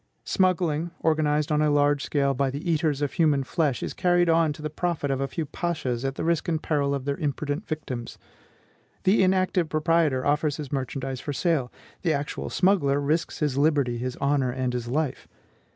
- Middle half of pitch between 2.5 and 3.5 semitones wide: Yes, average, 2.9 semitones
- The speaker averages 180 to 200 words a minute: Yes, average, 190 wpm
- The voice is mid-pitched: Yes, medium, 150 Hz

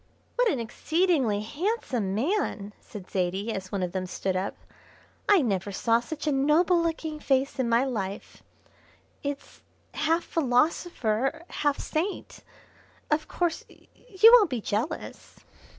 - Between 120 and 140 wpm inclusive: Yes, slow, 135 wpm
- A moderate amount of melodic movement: No, wide, 7.8 semitones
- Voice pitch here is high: Yes, very high, 270 Hz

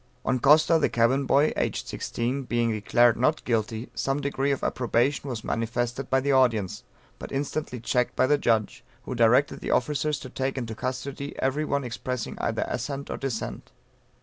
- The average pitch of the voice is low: Yes, low, 130 Hz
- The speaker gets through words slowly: No, average, 175 wpm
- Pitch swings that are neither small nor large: Yes, average, 3.0 semitones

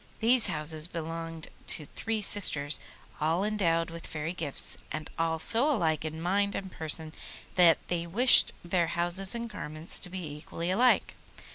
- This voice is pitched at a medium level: Yes, medium, 170 Hz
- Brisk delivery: No, average, 155 wpm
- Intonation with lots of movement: No, average, 3.7 semitones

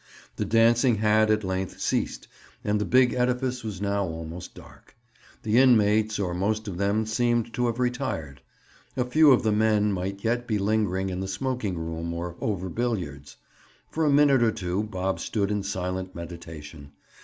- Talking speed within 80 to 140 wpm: No, average, 175 wpm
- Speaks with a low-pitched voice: Yes, low, 105 Hz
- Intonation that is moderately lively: Yes, average, 4.3 semitones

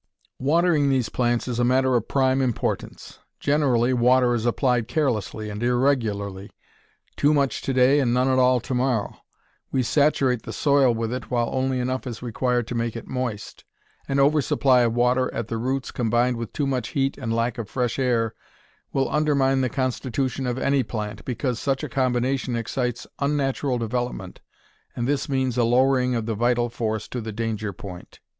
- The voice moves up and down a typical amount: No, narrow, 2.3 semitones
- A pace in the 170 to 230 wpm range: Yes, average, 180 wpm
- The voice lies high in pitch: No, low, 125 Hz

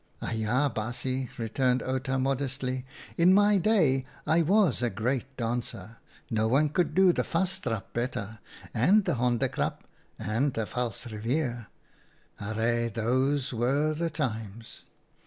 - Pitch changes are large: No, average, 4.1 semitones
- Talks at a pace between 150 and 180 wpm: No, average, 140 wpm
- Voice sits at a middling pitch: No, low, 130 Hz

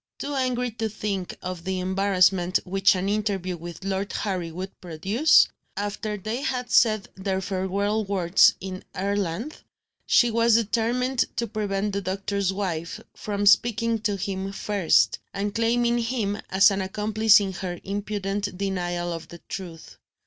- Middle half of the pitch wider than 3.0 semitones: No, narrow, 2.5 semitones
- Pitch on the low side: No, high, 200 Hz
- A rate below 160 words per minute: Yes, average, 150 wpm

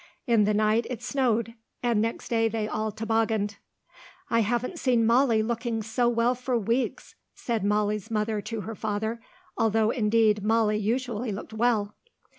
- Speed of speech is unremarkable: Yes, average, 155 wpm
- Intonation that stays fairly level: Yes, narrow, 1.8 semitones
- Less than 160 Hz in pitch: No, high, 225 Hz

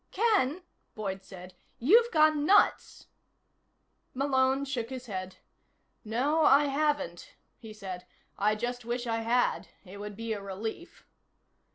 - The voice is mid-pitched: No, high, 240 Hz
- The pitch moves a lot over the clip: Yes, wide, 5.7 semitones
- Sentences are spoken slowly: Yes, slow, 130 wpm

